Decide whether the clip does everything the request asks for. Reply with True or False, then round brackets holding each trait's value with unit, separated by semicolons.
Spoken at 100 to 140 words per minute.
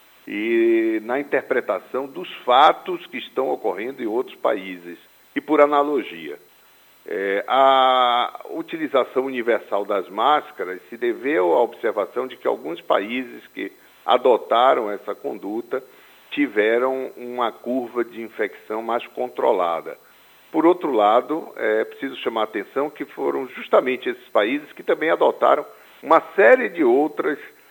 True (130 wpm)